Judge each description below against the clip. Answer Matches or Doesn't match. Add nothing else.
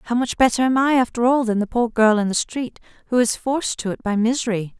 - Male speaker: Doesn't match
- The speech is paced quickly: Matches